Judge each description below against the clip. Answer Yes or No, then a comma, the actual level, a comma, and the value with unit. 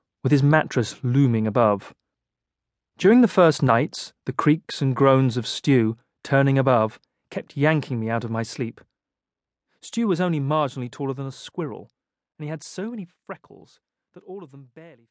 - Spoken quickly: No, average, 170 wpm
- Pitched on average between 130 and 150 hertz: Yes, medium, 140 Hz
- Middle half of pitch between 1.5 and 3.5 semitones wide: No, average, 4.7 semitones